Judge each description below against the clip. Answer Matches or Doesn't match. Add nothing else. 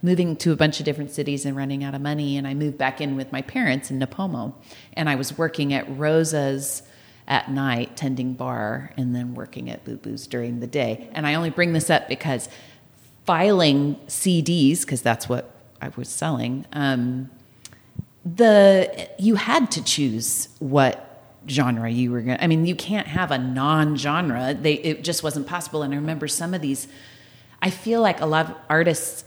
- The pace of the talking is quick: Doesn't match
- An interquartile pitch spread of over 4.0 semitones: Doesn't match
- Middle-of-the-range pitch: Matches